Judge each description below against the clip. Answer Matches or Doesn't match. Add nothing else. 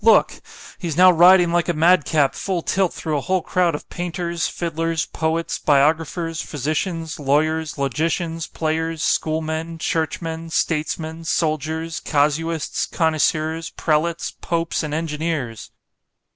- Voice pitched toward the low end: Doesn't match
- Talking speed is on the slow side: Matches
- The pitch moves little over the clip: Matches